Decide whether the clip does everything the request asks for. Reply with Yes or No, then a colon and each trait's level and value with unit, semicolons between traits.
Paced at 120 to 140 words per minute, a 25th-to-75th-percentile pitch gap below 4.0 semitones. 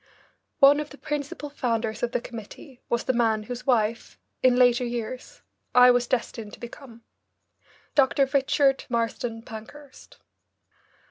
Yes: slow, 135 wpm; average, 2.8 semitones